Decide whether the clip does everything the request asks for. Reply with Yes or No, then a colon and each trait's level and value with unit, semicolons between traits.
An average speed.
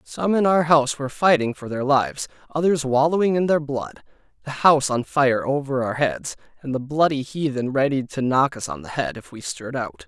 No: fast, 215 wpm